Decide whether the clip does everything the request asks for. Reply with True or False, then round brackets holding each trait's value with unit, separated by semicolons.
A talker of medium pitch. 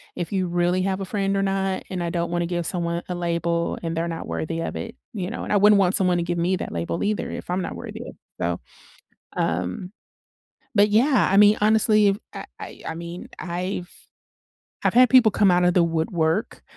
True (180 Hz)